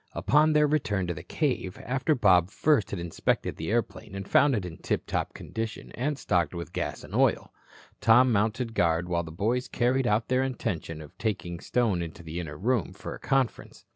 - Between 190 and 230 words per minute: Yes, average, 195 wpm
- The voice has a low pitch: Yes, low, 105 Hz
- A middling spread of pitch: No, wide, 6.5 semitones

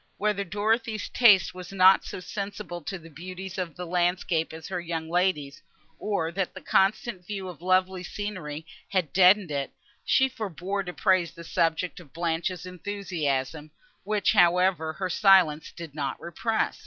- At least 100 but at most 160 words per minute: Yes, average, 155 wpm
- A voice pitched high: No, medium, 180 Hz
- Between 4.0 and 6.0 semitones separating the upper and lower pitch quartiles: No, average, 2.9 semitones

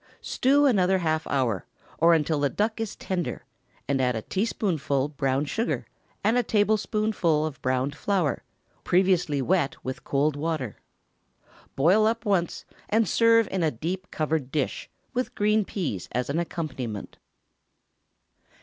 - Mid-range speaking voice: Yes, medium, 165 Hz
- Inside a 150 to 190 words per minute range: No, average, 140 wpm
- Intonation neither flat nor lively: No, wide, 6.7 semitones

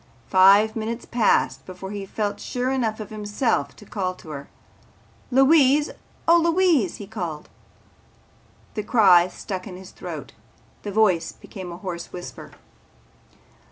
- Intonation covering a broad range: No, average, 4.2 semitones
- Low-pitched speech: No, high, 205 Hz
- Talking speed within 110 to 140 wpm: Yes, slow, 135 wpm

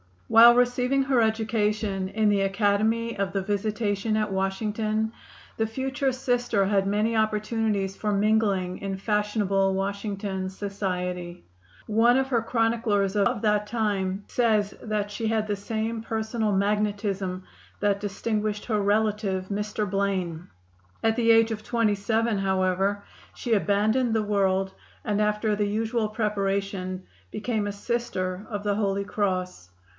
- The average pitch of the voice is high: Yes, high, 210 Hz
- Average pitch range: No, narrow, 2.0 semitones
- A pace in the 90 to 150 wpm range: Yes, slow, 135 wpm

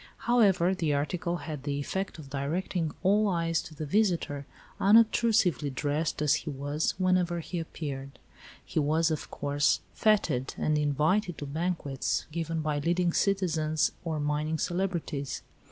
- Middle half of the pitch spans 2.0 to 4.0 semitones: Yes, average, 3.7 semitones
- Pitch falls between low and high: Yes, medium, 160 Hz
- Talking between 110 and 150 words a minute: Yes, average, 140 wpm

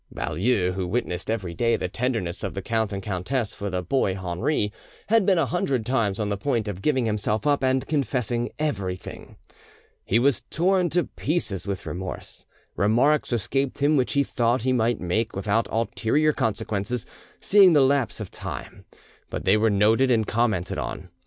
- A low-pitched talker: Yes, low, 115 Hz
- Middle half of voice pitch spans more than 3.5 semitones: Yes, average, 5.1 semitones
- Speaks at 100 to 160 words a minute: No, average, 175 wpm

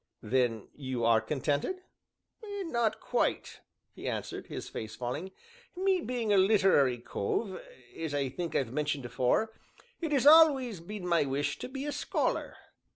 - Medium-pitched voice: Yes, medium, 170 Hz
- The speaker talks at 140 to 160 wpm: Yes, average, 150 wpm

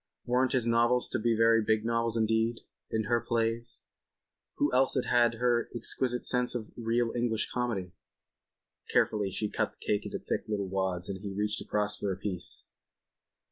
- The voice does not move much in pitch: Yes, narrow, 2.3 semitones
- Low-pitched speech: Yes, low, 115 Hz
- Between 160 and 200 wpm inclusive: Yes, average, 170 wpm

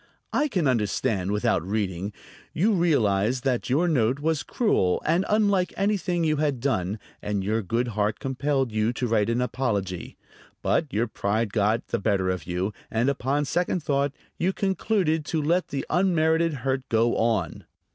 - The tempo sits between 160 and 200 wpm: Yes, average, 165 wpm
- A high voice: No, low, 130 Hz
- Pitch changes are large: Yes, wide, 7.1 semitones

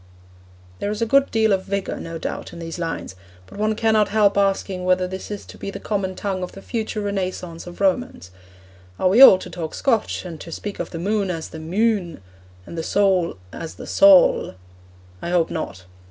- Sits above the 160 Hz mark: Yes, high, 190 Hz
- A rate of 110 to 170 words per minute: No, fast, 205 wpm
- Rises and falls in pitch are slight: No, average, 3.4 semitones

